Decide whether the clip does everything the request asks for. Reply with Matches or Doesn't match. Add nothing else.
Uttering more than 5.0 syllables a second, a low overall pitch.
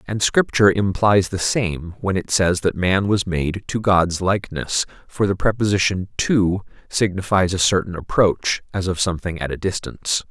Doesn't match